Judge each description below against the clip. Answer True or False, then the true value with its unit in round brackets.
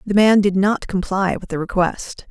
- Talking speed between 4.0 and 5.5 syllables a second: True (4.6 syllables/s)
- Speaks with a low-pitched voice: False (195 Hz)